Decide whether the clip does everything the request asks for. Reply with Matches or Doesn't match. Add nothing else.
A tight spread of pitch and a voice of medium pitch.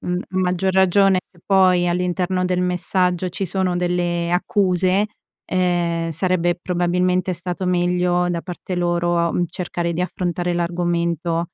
Matches